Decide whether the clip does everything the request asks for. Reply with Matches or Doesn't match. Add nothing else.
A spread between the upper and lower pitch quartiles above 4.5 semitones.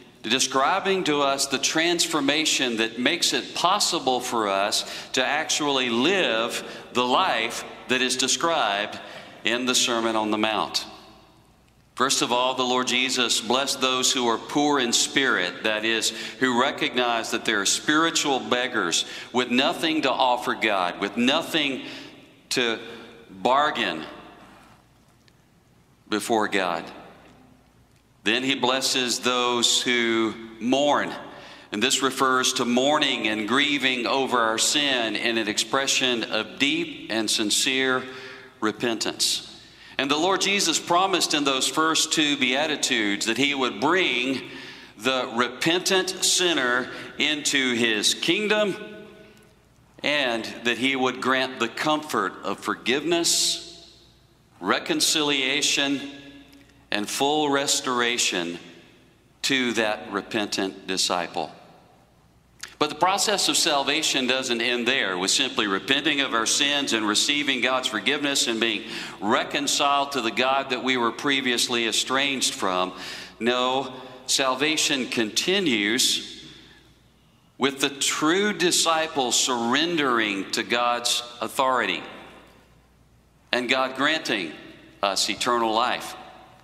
Doesn't match